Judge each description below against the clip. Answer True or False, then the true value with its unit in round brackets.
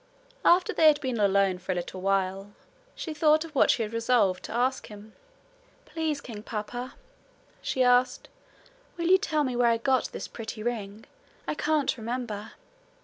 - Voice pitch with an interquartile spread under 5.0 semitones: False (5.5 semitones)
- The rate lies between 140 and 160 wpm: False (170 wpm)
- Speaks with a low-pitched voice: False (240 Hz)